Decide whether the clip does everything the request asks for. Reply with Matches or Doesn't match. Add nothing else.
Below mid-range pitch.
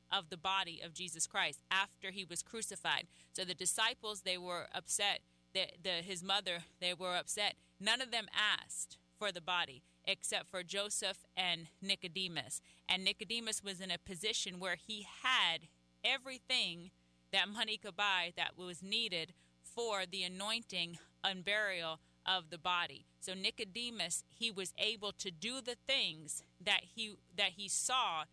Doesn't match